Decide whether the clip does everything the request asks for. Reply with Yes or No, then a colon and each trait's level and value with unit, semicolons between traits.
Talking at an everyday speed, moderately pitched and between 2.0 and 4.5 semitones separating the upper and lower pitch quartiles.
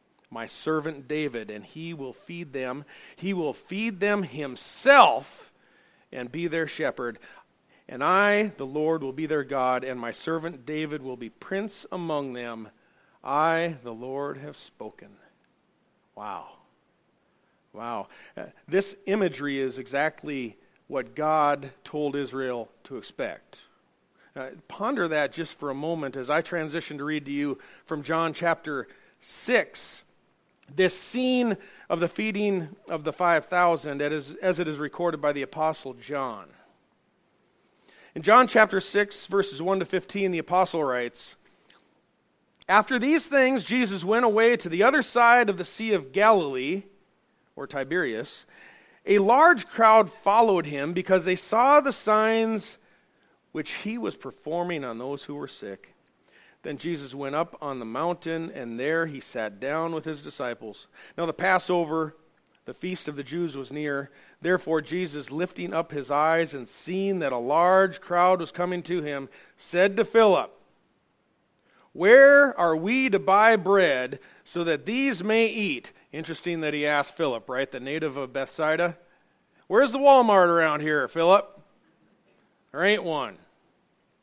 No: average, 145 wpm; medium, 165 Hz; average, 5.2 semitones